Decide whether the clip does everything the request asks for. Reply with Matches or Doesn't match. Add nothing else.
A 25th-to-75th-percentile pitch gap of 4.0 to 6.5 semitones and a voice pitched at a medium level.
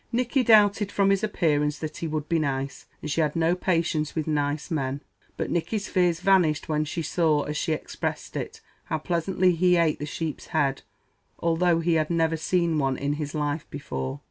Doesn't match